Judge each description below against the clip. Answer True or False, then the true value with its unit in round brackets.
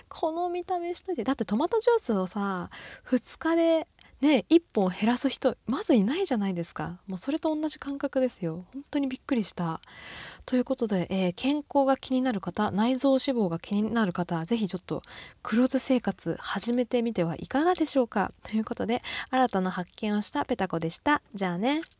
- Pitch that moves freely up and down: True (6.2 semitones)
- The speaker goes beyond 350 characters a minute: True (375 characters per minute)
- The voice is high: True (245 Hz)